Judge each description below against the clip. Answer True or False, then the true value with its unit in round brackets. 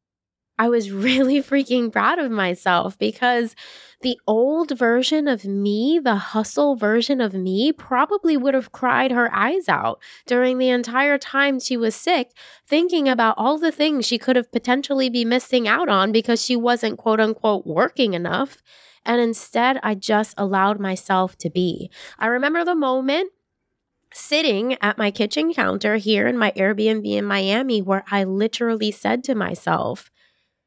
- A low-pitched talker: False (240 Hz)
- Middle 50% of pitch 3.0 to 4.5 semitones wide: True (4.2 semitones)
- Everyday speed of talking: True (160 wpm)